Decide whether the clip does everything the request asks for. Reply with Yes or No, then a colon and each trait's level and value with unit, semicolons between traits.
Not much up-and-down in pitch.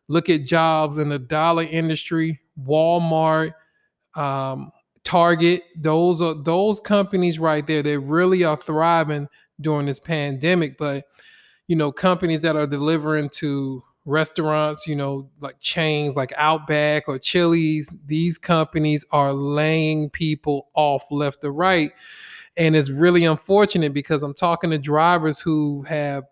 Yes: narrow, 2.3 semitones